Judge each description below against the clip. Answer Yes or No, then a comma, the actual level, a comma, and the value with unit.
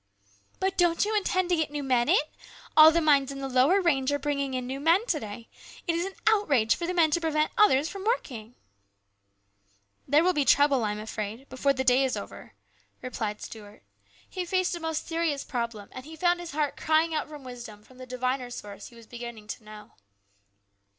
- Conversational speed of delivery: No, fast, 215 wpm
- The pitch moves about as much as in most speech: No, wide, 5.9 semitones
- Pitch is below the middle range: No, very high, 275 Hz